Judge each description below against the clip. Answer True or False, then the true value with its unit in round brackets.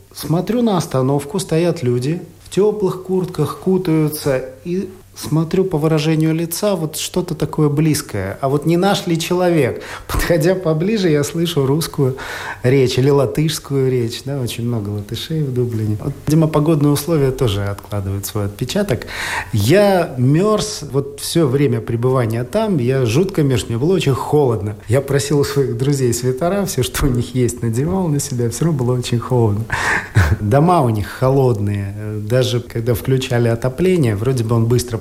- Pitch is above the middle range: False (140 Hz)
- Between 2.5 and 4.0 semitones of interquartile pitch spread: False (5.3 semitones)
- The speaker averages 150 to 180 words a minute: True (155 wpm)